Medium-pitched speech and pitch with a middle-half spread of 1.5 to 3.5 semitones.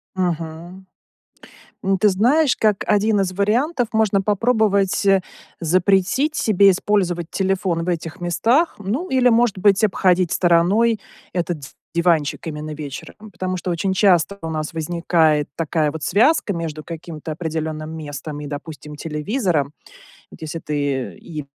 No: medium, 180 Hz; average, 4.3 semitones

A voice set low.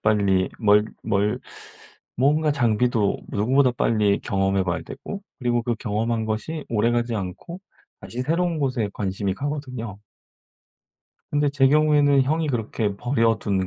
Yes: low, 120 Hz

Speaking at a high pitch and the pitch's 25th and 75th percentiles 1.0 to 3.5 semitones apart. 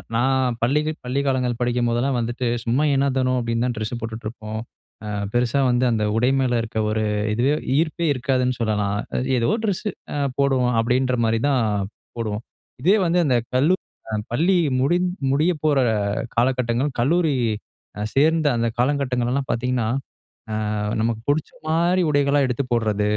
No: low, 125 Hz; average, 3.1 semitones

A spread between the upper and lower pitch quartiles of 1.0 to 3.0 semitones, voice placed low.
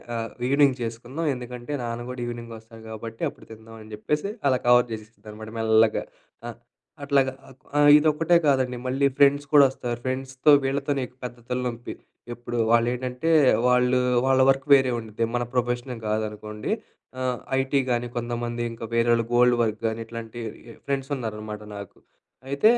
Yes: average, 2.7 semitones; low, 120 Hz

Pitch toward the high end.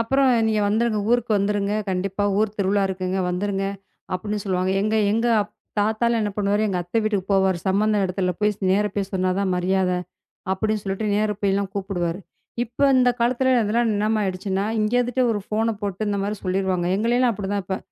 Yes: high, 205 Hz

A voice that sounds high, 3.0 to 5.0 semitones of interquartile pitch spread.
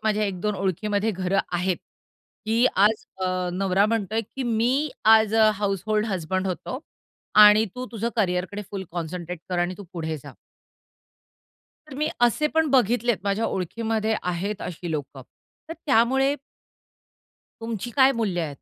Yes: high, 210 Hz; average, 3.7 semitones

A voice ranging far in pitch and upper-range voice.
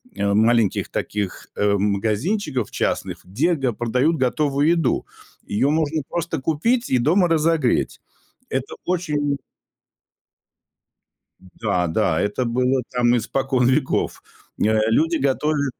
No: wide, 5.8 semitones; low, 130 Hz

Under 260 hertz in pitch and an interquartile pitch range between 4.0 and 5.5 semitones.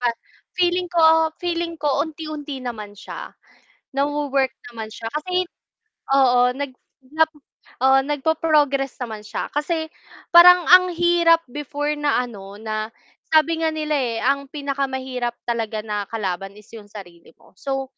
No: very high, 280 Hz; average, 5.1 semitones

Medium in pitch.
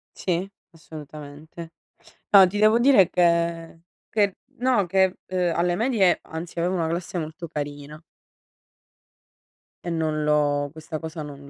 Yes: medium, 170 Hz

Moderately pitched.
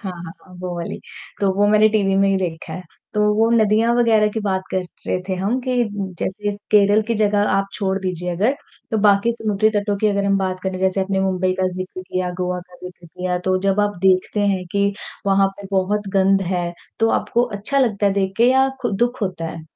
No: high, 195 Hz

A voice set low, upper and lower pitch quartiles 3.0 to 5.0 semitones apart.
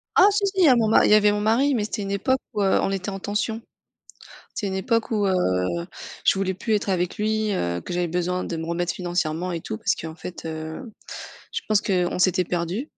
No: high, 195 Hz; average, 3.6 semitones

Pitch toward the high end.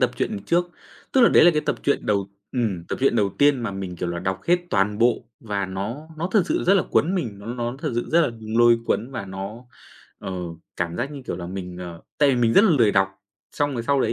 No: low, 115 Hz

